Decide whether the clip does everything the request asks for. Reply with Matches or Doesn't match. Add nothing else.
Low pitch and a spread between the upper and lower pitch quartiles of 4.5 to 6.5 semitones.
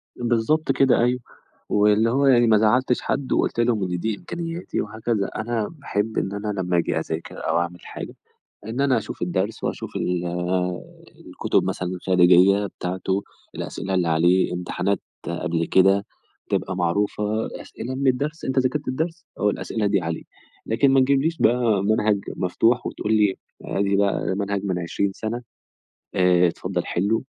Matches